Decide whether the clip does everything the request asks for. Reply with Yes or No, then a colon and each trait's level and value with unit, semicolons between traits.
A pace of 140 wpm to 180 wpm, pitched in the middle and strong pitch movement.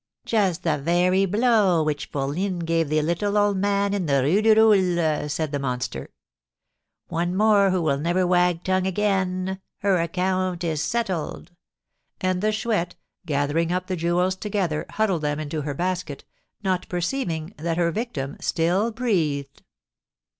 No: average, 150 wpm; medium, 180 Hz; average, 3.7 semitones